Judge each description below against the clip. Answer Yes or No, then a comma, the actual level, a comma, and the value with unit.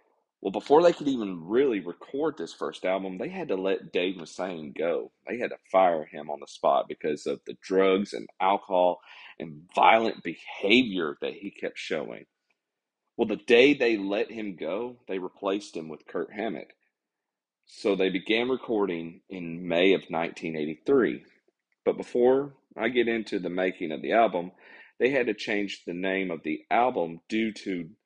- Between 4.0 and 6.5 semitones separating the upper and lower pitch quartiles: Yes, average, 4.3 semitones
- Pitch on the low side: Yes, very low, 95 Hz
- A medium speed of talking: Yes, average, 170 wpm